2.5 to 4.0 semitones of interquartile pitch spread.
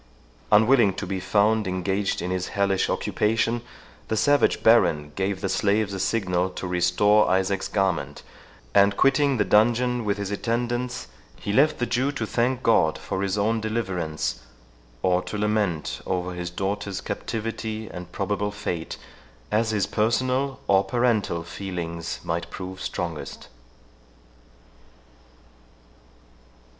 Yes: average, 3.5 semitones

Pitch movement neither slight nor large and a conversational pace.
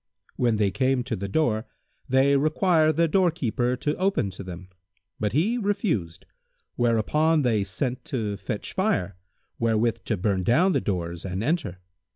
No: wide, 7.7 semitones; average, 155 wpm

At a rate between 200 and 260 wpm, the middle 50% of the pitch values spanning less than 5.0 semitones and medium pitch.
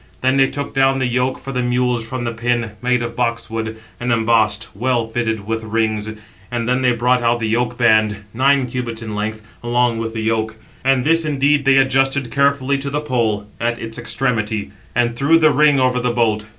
No: fast, 205 wpm; average, 2.7 semitones; low, 120 Hz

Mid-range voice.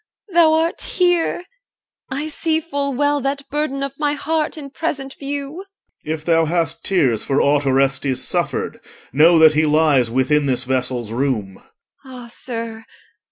No: high, 225 Hz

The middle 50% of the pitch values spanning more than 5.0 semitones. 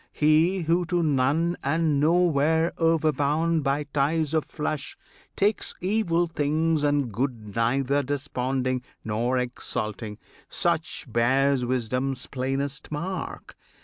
No: average, 4.0 semitones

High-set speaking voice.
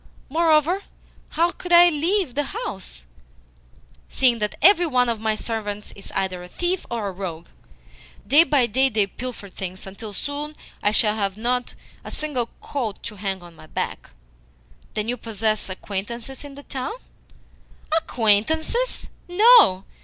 Yes: high, 235 Hz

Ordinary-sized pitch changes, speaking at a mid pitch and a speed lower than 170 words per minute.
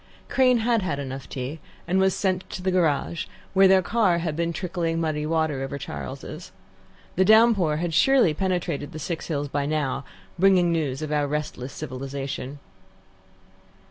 Yes: average, 4.6 semitones; medium, 165 Hz; average, 160 wpm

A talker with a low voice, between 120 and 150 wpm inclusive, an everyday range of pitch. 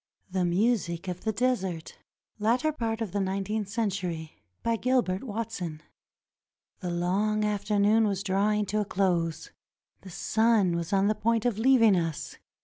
No: high, 205 Hz; average, 140 wpm; average, 3.5 semitones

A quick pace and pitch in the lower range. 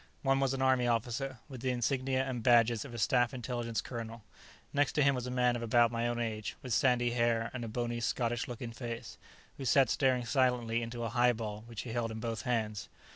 Yes: fast, 220 wpm; low, 120 Hz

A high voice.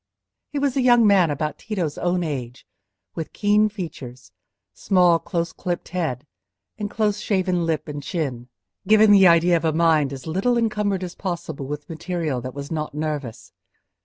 No: medium, 170 Hz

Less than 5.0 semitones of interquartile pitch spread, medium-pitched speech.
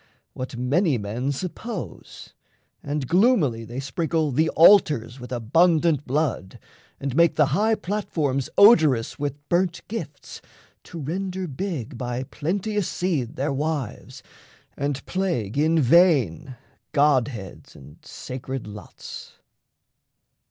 No: average, 5.3 semitones; medium, 145 Hz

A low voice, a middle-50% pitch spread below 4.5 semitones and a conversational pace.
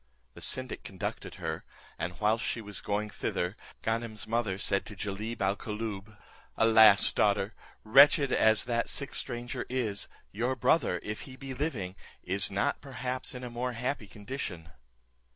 Yes: low, 110 Hz; average, 3.7 semitones; average, 150 wpm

